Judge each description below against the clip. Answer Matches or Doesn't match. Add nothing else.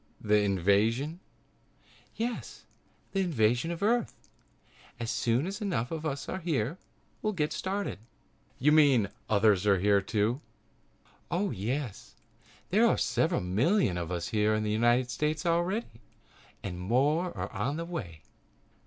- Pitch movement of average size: Doesn't match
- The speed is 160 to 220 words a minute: Doesn't match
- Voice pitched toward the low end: Matches